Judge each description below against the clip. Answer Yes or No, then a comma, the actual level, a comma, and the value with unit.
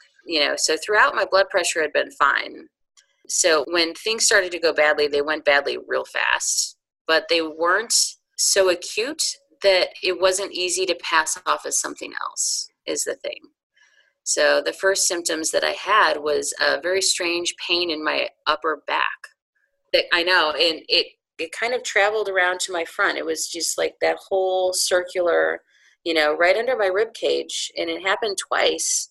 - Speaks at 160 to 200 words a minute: Yes, average, 180 wpm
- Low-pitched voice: No, medium, 185 Hz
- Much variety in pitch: Yes, wide, 7.2 semitones